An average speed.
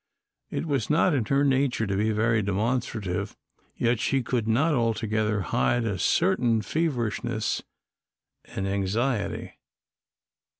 No: slow, 120 wpm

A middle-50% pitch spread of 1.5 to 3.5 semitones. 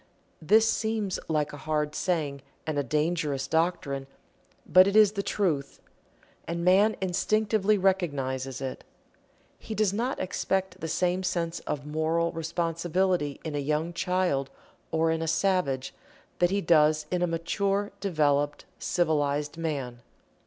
No: average, 4.1 semitones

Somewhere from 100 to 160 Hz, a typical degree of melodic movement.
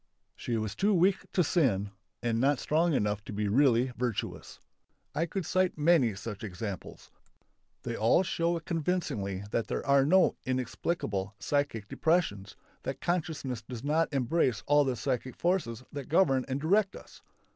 No: low, 135 Hz; wide, 6.7 semitones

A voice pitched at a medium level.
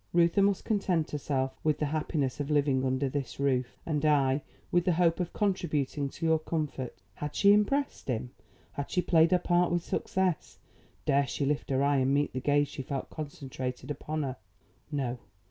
Yes: medium, 145 Hz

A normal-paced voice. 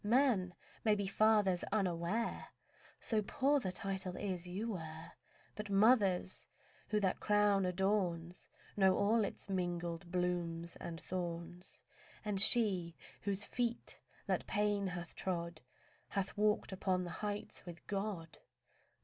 No: slow, 125 wpm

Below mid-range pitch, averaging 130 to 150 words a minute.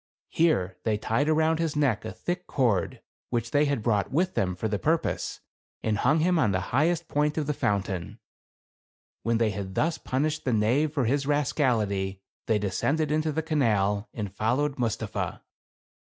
No: low, 130 Hz; average, 175 wpm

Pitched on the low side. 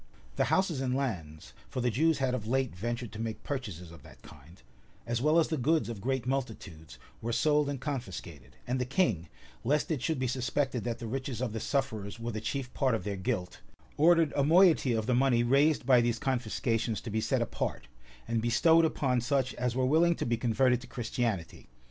Yes: low, 125 Hz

